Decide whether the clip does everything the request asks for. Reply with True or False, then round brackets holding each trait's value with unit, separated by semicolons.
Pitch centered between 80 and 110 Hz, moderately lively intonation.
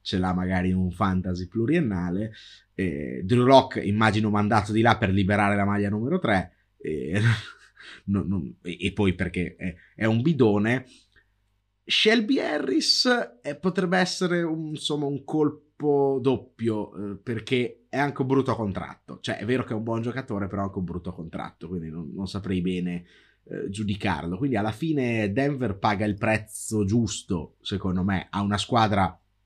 True (105 Hz; 4.8 semitones)